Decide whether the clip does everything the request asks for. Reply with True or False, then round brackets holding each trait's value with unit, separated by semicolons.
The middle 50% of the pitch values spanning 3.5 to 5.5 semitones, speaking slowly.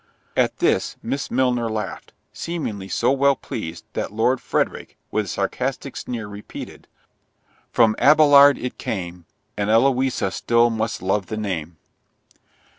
True (4.4 semitones; 130 wpm)